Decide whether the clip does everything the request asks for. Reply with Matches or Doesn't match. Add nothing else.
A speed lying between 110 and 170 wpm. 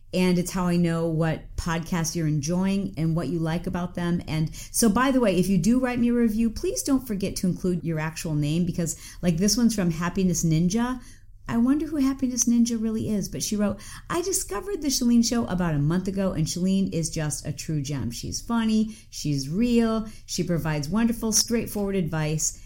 Doesn't match